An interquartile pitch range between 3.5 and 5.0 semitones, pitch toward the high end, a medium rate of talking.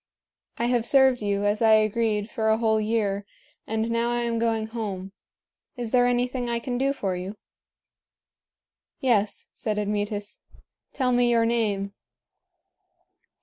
No: narrow, 2.5 semitones; high, 225 Hz; average, 145 wpm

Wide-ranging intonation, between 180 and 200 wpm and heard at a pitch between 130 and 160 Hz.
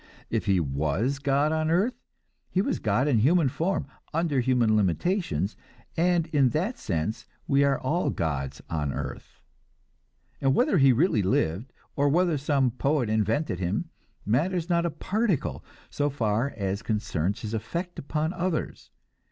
No: wide, 7.6 semitones; average, 150 wpm; low, 135 Hz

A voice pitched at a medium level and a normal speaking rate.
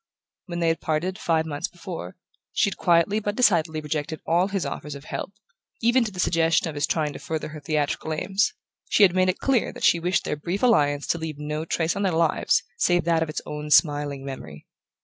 No: medium, 165 Hz; fast, 220 wpm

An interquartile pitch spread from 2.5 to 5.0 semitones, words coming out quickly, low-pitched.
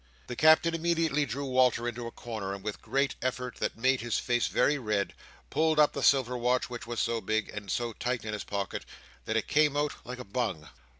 Yes: average, 3.8 semitones; fast, 225 wpm; low, 125 Hz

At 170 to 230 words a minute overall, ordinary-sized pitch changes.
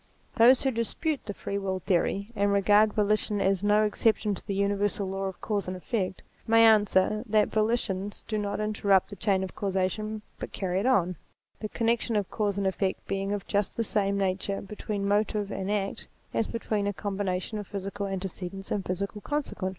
No: average, 195 wpm; narrow, 1.6 semitones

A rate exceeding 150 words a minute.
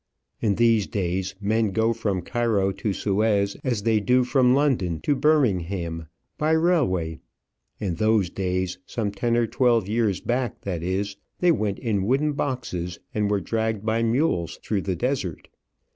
Yes: average, 160 wpm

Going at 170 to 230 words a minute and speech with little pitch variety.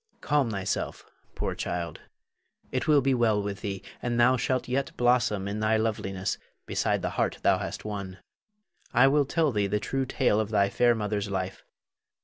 No: average, 180 wpm; average, 4.0 semitones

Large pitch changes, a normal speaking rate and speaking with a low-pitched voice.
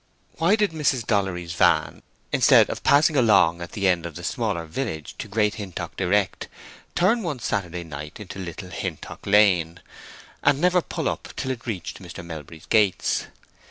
Yes: wide, 6.9 semitones; average, 165 wpm; low, 100 Hz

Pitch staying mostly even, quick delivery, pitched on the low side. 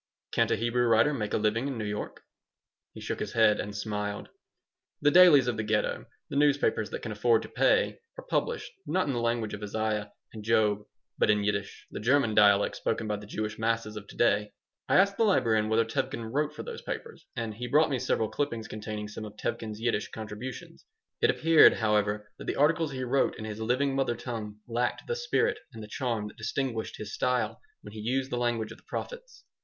No: average, 3.9 semitones; fast, 215 wpm; low, 115 Hz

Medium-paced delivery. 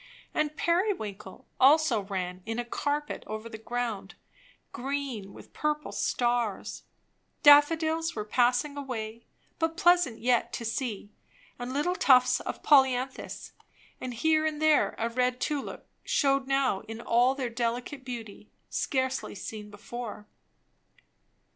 No: slow, 125 wpm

